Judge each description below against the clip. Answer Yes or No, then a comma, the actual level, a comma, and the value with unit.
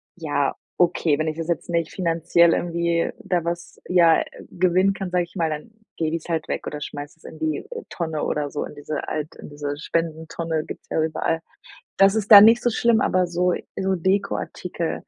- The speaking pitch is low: No, medium, 170 Hz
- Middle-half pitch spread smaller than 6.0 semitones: Yes, narrow, 2.4 semitones